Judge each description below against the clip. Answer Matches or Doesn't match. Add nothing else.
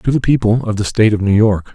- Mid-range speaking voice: Doesn't match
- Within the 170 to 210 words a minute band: Doesn't match